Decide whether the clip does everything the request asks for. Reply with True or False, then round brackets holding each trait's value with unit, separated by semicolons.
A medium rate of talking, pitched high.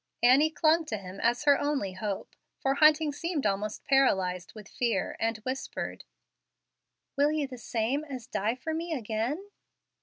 True (155 wpm; 255 Hz)